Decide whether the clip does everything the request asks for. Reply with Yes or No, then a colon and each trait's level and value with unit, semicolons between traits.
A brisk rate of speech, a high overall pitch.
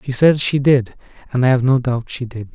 No: fast, 260 wpm; low, 130 Hz